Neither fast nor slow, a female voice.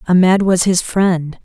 Yes: average, 165 wpm; female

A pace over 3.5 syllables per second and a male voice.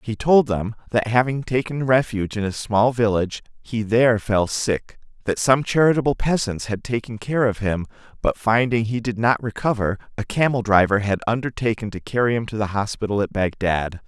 Yes: 5.3 syllables/s; male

